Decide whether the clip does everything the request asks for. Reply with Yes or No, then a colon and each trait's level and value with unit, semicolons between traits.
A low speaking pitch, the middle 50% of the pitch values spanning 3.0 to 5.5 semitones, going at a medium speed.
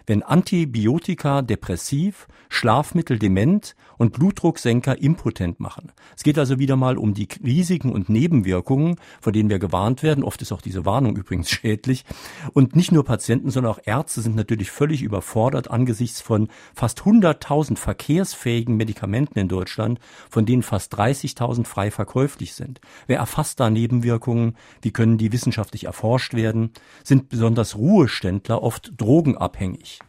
Yes: low, 120 Hz; average, 4.2 semitones; average, 145 wpm